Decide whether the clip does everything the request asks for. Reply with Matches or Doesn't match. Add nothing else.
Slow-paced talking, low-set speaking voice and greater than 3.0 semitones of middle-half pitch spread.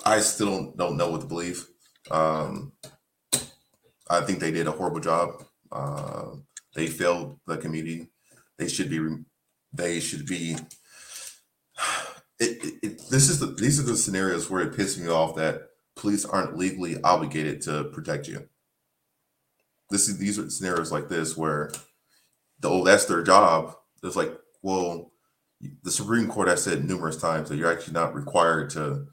Doesn't match